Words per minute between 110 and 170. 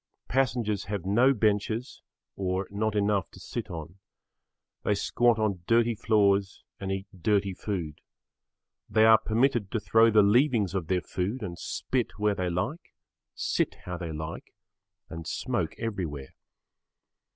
Yes: average, 140 wpm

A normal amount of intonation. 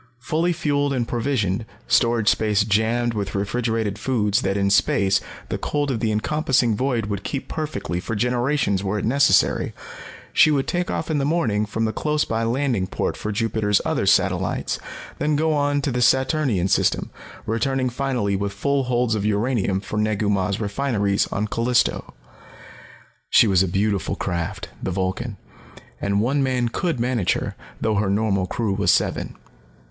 Yes: average, 4.7 semitones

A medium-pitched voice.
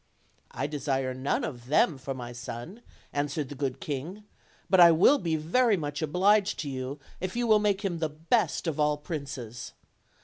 Yes: medium, 150 Hz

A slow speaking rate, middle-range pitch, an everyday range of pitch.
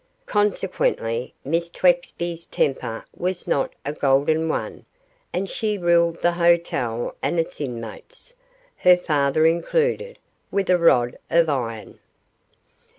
Yes: slow, 115 wpm; medium, 170 Hz; average, 4.5 semitones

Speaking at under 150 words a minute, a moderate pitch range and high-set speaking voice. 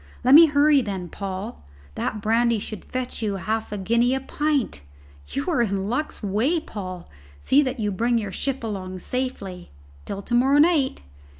No: average, 175 wpm; average, 5.0 semitones; high, 230 Hz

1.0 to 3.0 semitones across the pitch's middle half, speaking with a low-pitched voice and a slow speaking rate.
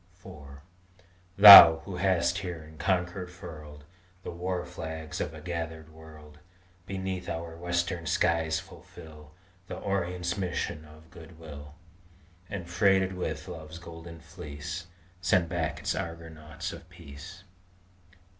Yes: narrow, 2.5 semitones; very low, 85 Hz; slow, 125 wpm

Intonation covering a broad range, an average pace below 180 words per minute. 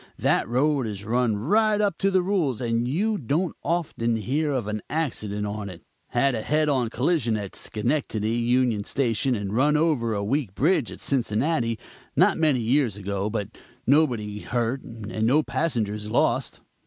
Yes: wide, 5.8 semitones; average, 165 wpm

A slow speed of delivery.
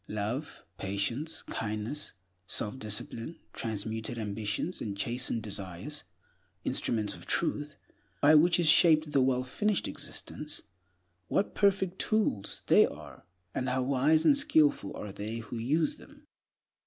Yes: slow, 120 wpm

